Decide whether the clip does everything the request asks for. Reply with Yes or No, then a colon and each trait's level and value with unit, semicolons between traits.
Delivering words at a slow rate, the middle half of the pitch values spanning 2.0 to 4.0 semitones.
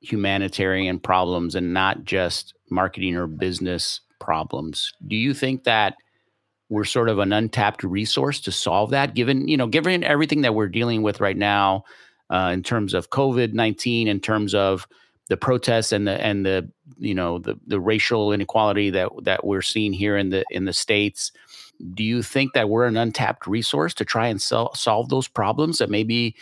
No: average, 180 wpm; average, 3.6 semitones